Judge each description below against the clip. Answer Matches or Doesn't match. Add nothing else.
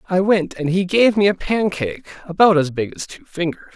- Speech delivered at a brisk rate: Matches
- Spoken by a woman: Doesn't match